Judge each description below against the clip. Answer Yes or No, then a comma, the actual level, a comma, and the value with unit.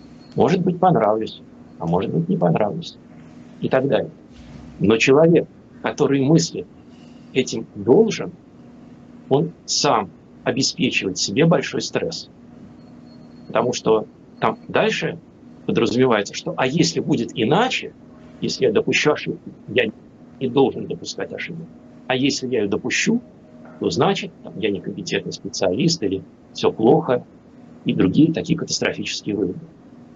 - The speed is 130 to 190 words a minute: No, average, 120 wpm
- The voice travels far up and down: Yes, wide, 6.2 semitones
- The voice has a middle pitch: No, low, 130 Hz